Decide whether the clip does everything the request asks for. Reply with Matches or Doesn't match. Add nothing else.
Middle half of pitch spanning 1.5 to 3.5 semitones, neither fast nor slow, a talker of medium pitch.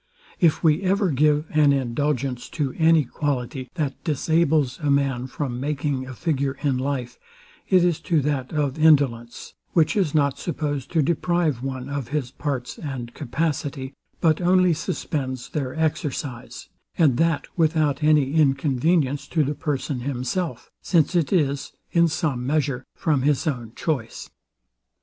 Matches